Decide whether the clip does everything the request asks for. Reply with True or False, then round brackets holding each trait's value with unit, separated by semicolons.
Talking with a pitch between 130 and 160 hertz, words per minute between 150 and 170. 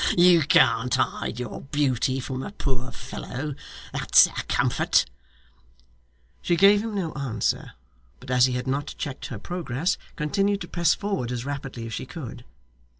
True (135 Hz; 160 wpm)